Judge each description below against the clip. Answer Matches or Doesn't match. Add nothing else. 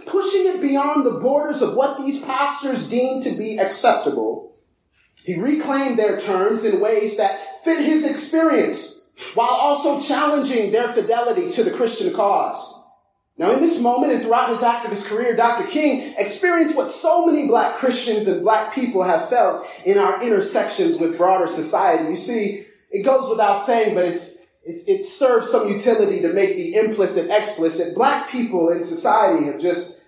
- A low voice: Doesn't match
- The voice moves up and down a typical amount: Doesn't match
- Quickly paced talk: Doesn't match